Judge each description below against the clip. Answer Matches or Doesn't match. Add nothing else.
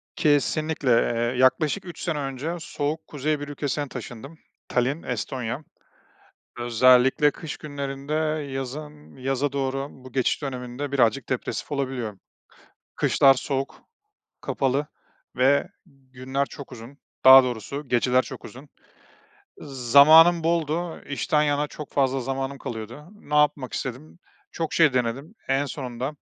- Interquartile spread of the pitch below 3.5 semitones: Matches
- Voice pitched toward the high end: Doesn't match